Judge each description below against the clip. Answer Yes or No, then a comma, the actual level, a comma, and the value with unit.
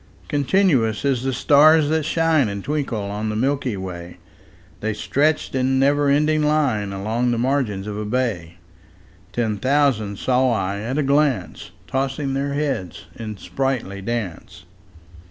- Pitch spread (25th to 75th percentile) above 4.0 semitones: Yes, wide, 5.4 semitones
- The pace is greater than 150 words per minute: No, average, 145 wpm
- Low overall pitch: Yes, low, 130 Hz